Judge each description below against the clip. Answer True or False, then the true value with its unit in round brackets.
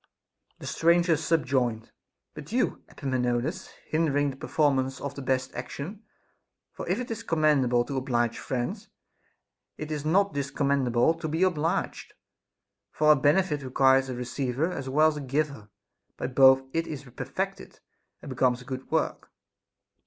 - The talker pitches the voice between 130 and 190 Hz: True (140 Hz)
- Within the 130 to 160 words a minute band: True (150 wpm)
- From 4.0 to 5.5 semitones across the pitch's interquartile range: False (3.3 semitones)